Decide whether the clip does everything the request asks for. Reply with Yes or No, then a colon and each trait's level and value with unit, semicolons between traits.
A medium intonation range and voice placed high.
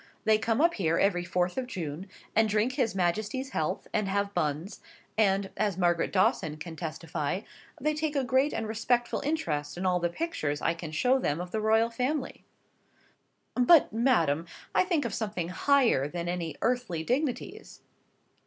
No: wide, 6.5 semitones; high, 200 Hz